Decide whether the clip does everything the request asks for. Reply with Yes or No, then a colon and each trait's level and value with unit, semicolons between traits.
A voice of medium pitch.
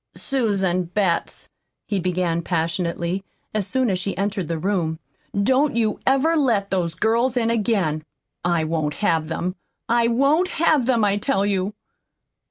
No: high, 200 Hz